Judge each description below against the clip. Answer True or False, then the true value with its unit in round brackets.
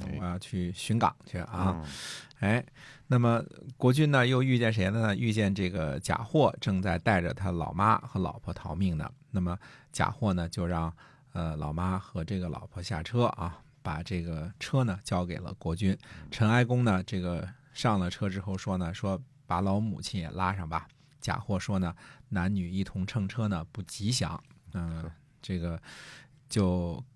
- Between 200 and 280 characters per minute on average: True (235 characters per minute)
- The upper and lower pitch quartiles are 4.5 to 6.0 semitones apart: True (5.3 semitones)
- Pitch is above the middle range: False (95 Hz)